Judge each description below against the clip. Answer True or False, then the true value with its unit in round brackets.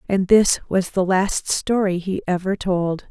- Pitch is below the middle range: False (190 Hz)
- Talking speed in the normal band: True (175 wpm)